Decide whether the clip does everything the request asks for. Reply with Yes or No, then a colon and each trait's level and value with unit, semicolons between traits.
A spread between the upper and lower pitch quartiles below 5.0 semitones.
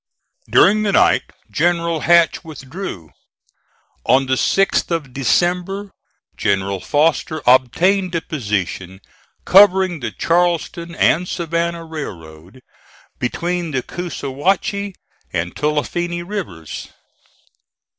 No: wide, 5.5 semitones